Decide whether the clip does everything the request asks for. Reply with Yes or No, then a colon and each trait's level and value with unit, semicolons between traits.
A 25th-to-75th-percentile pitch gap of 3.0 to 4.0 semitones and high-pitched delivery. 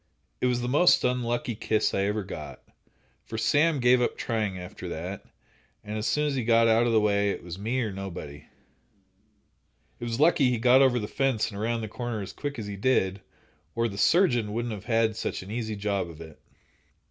No: average, 3.4 semitones; low, 115 Hz